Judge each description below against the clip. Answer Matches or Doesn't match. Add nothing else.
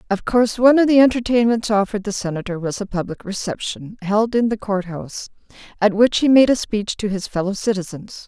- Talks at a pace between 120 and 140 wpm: Doesn't match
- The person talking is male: Doesn't match